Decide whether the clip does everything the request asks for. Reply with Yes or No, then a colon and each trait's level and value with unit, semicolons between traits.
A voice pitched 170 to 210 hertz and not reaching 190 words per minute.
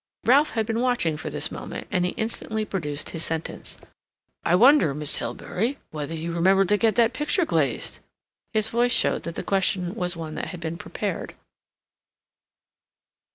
Yes: high, 190 Hz; average, 165 wpm